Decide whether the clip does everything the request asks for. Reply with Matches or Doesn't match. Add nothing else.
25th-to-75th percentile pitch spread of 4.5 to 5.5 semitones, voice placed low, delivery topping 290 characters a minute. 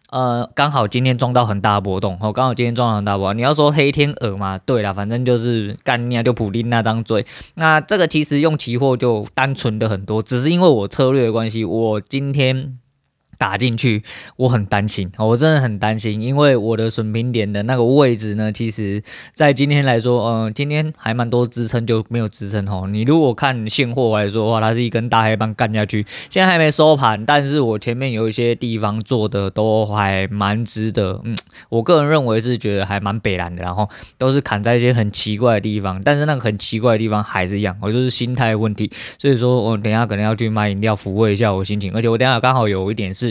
Doesn't match